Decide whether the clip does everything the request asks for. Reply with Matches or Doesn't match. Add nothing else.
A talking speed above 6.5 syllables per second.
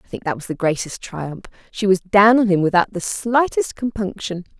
Doesn't match